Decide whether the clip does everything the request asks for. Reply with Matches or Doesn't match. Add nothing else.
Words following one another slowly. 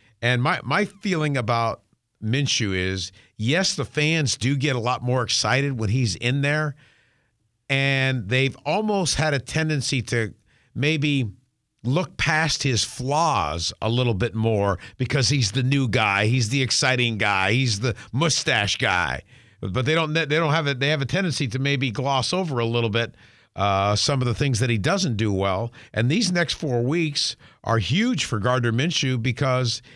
Doesn't match